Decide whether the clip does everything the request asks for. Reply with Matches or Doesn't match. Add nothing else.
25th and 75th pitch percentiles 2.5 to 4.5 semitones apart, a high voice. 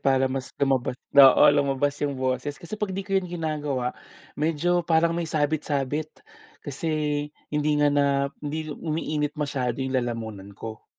Doesn't match